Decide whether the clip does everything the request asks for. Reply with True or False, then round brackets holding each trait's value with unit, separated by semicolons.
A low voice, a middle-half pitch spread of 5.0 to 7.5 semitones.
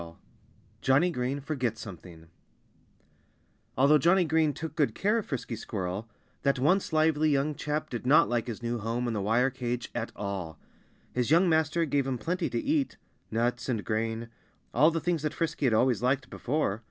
True (130 Hz; 5.3 semitones)